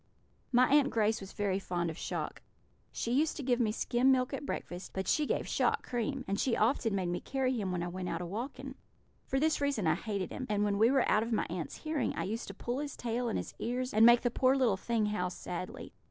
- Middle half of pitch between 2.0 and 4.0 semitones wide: No, average, 4.9 semitones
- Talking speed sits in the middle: No, fast, 250 wpm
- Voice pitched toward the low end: No, high, 230 Hz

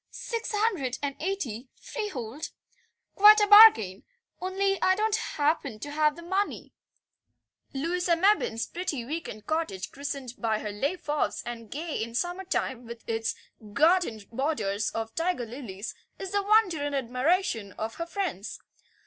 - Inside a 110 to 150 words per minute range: Yes, average, 145 wpm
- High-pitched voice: Yes, very high, 295 Hz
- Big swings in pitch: Yes, wide, 8.2 semitones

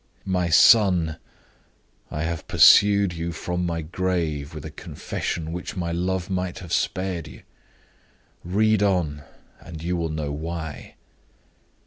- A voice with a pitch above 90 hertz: No, very low, 85 Hz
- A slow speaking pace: Yes, slow, 130 wpm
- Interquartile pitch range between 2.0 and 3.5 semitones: Yes, narrow, 2.6 semitones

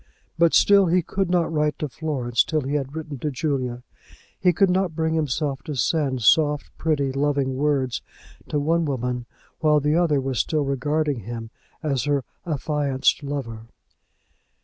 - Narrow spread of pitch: No, average, 3.1 semitones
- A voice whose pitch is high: No, medium, 145 Hz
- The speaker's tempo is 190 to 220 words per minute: No, average, 160 wpm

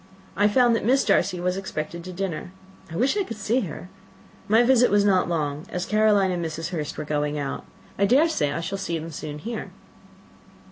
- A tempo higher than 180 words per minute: Yes, fast, 205 wpm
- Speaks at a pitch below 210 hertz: Yes, medium, 185 Hz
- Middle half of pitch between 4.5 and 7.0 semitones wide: Yes, average, 5.0 semitones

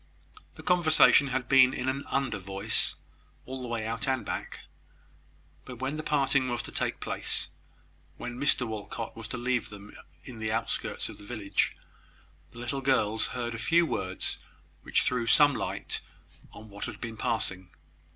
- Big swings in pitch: No, average, 3.2 semitones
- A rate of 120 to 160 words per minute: No, average, 170 wpm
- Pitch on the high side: No, low, 120 Hz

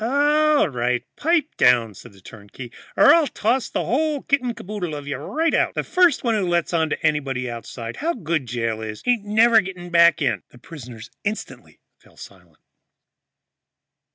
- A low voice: No, medium, 170 Hz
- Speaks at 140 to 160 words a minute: No, average, 180 wpm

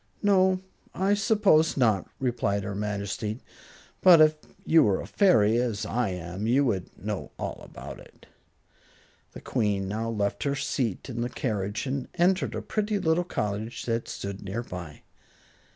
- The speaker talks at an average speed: Yes, average, 155 wpm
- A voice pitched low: Yes, low, 115 Hz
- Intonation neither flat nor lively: No, wide, 7.6 semitones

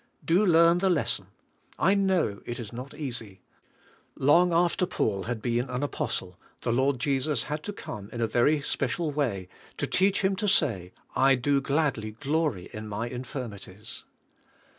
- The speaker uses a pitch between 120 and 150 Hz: Yes, low, 135 Hz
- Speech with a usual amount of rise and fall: No, wide, 5.9 semitones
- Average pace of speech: Yes, average, 160 wpm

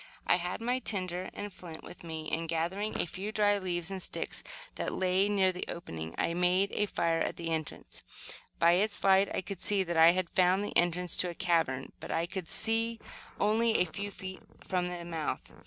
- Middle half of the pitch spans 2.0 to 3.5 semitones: Yes, average, 2.9 semitones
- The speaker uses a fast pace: Yes, fast, 210 wpm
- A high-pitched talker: No, medium, 180 Hz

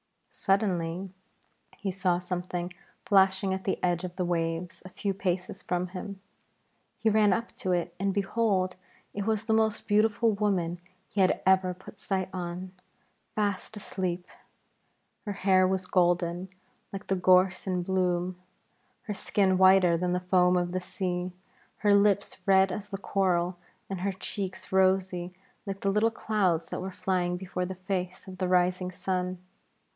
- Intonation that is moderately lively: No, narrow, 1.5 semitones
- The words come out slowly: No, average, 160 wpm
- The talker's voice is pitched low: No, medium, 185 Hz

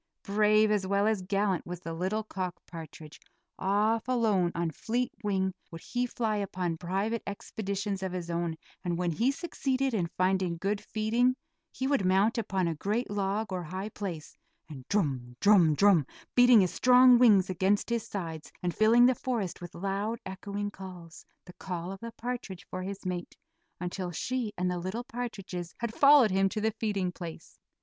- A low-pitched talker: No, high, 195 Hz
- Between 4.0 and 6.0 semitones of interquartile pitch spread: No, average, 3.6 semitones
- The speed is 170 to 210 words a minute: Yes, average, 175 wpm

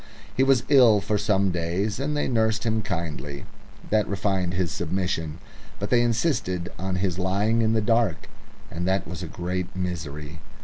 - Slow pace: No, average, 170 wpm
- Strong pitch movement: No, average, 4.0 semitones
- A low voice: Yes, very low, 95 Hz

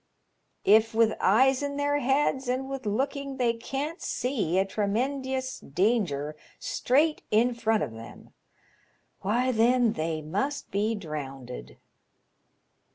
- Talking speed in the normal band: No, slow, 125 wpm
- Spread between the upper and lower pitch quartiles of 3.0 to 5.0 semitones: No, wide, 5.4 semitones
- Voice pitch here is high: Yes, high, 230 Hz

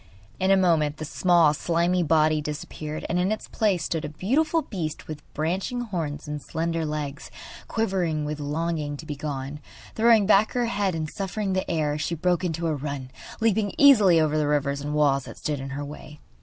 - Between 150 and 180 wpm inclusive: No, average, 195 wpm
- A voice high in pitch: No, medium, 160 Hz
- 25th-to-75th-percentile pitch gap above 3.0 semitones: Yes, average, 4.1 semitones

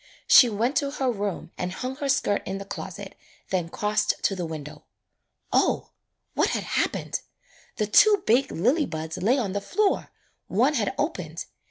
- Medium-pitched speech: No, high, 210 Hz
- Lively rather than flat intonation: Yes, wide, 6.0 semitones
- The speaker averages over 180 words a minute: No, average, 170 wpm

